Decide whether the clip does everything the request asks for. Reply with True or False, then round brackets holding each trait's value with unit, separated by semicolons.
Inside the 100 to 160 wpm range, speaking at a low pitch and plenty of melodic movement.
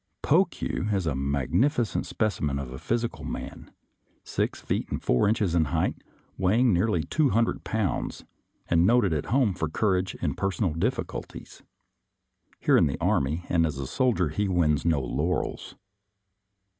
True (155 wpm; 90 Hz; 6.1 semitones)